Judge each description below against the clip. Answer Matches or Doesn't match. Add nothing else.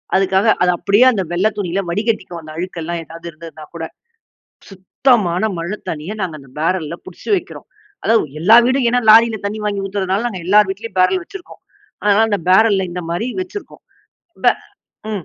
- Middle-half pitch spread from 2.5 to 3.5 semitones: Doesn't match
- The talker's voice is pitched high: Matches